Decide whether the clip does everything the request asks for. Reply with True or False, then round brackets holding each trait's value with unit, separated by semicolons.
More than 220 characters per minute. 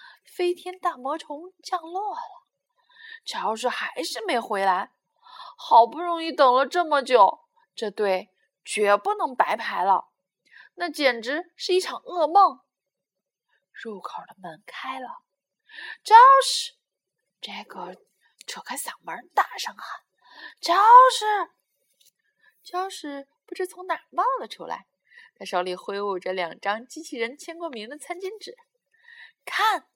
False (180 characters per minute)